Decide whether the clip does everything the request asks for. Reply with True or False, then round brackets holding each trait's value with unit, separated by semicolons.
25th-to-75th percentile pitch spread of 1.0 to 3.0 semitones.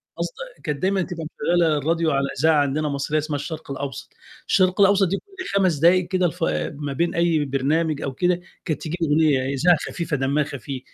False (3.7 semitones)